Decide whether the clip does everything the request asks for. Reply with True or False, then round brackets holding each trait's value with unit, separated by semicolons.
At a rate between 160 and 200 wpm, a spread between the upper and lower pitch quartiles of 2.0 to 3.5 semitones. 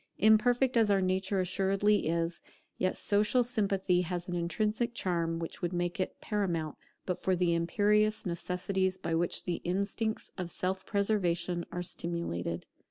False (150 wpm; 3.1 semitones)